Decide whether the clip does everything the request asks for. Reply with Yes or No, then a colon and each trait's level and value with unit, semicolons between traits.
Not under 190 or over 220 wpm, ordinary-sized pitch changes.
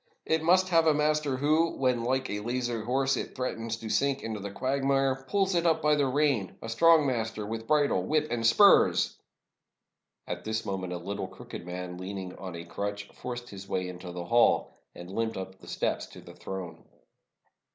No: average, 195 wpm; wide, 6.6 semitones